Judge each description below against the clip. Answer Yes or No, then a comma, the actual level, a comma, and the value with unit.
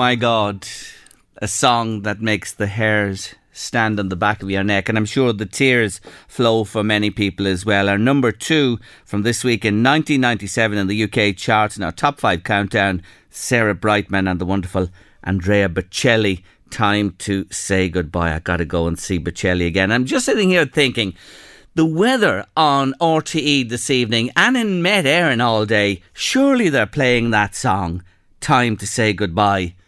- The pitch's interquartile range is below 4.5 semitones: Yes, average, 4.1 semitones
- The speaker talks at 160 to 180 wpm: Yes, average, 175 wpm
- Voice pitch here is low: Yes, low, 105 Hz